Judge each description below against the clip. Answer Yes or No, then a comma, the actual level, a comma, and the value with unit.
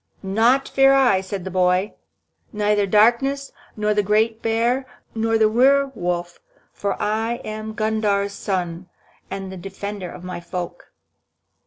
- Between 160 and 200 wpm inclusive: No, average, 140 wpm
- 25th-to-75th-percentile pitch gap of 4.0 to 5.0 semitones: No, average, 3.1 semitones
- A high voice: Yes, high, 210 Hz